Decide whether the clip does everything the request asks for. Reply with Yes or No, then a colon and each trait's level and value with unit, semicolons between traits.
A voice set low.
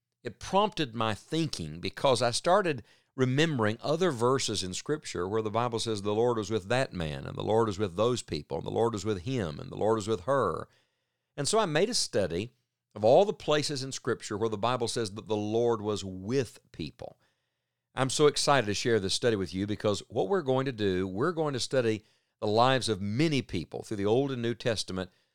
Yes: low, 115 Hz